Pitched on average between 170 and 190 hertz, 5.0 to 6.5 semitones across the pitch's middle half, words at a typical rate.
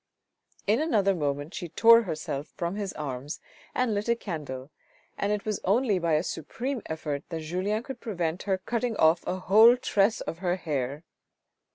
Yes: medium, 185 Hz; wide, 5.5 semitones; average, 180 wpm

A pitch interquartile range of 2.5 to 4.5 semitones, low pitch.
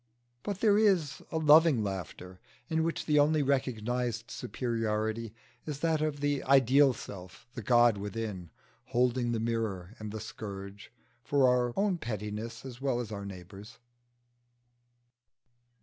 No: average, 5.1 semitones; low, 120 Hz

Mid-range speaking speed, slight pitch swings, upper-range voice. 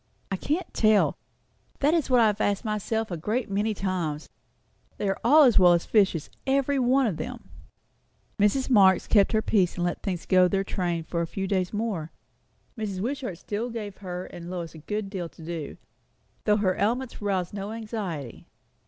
No: average, 190 wpm; average, 3.9 semitones; high, 200 Hz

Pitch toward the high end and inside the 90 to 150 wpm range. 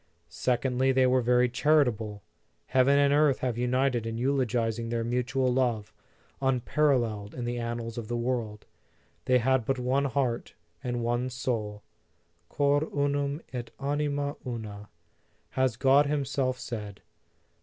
No: low, 125 Hz; slow, 135 wpm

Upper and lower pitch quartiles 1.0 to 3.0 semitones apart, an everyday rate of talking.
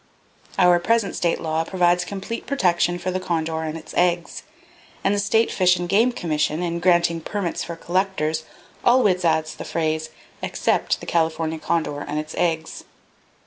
Yes: narrow, 2.5 semitones; average, 155 wpm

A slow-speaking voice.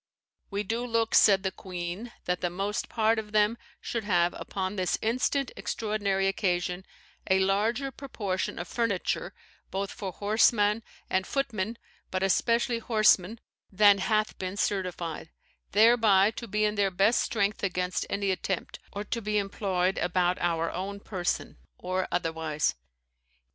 No: average, 145 wpm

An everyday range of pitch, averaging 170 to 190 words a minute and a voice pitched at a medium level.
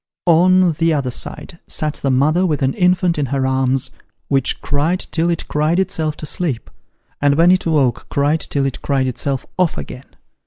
Yes: average, 3.8 semitones; average, 185 wpm; medium, 150 Hz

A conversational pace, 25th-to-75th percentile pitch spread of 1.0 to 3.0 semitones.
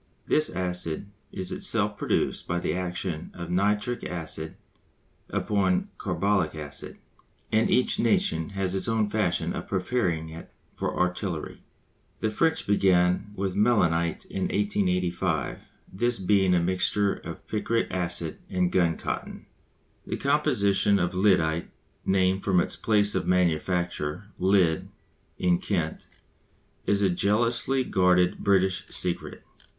No: slow, 125 wpm; average, 2.7 semitones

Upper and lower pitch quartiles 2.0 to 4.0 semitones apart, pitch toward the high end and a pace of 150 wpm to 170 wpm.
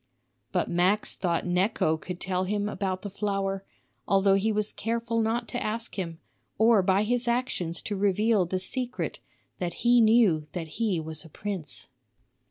Yes: average, 3.5 semitones; high, 200 Hz; average, 165 wpm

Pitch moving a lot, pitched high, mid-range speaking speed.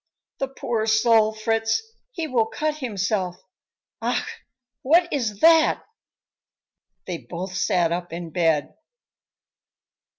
No: wide, 6.1 semitones; high, 220 Hz; slow, 105 wpm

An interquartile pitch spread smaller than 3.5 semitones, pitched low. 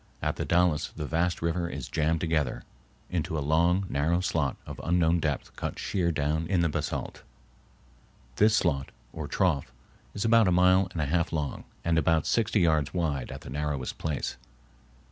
Yes: average, 2.9 semitones; very low, 80 Hz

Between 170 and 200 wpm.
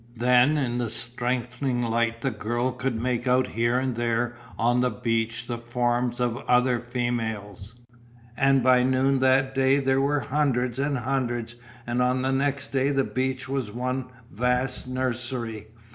No: average, 160 wpm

